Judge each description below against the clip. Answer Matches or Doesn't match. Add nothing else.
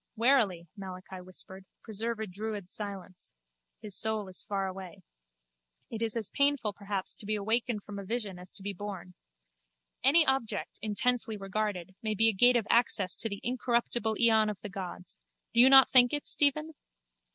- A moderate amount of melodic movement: Matches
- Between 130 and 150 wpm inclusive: Doesn't match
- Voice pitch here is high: Matches